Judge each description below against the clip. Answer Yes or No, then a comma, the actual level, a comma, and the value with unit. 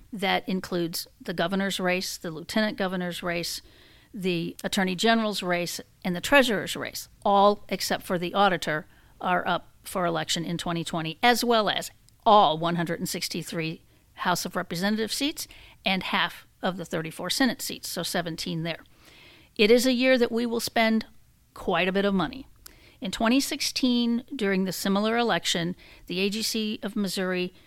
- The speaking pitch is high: Yes, high, 195 Hz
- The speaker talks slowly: No, average, 150 wpm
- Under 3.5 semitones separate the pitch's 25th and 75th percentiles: No, average, 4.1 semitones